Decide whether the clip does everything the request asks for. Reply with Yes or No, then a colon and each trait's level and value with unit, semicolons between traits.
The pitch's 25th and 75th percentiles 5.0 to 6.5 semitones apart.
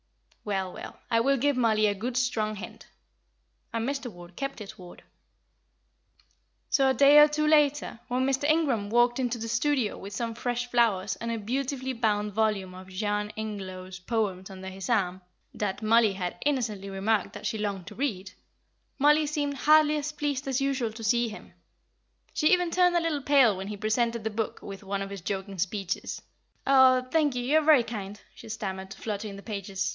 Yes: wide, 5.4 semitones